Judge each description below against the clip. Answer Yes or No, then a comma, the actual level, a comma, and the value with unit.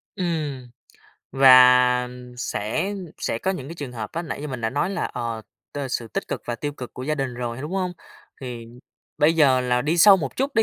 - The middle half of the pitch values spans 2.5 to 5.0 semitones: Yes, average, 4.7 semitones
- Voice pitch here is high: No, low, 130 Hz